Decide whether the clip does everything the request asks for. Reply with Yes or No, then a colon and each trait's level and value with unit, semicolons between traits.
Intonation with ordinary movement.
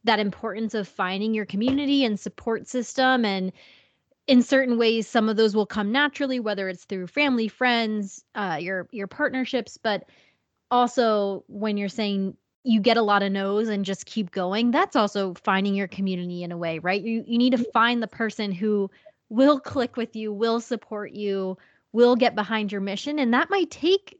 Yes: average, 3.6 semitones